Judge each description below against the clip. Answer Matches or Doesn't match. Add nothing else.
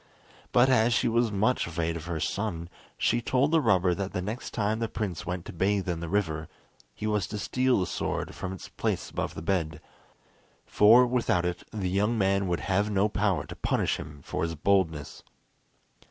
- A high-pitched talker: Doesn't match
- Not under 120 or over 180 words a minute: Doesn't match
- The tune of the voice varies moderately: Matches